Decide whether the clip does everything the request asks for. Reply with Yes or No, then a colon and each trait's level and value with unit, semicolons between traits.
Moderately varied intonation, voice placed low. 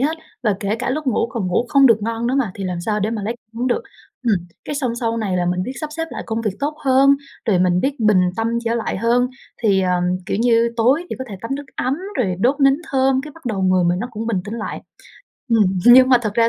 No: average, 4.5 semitones; high, 230 Hz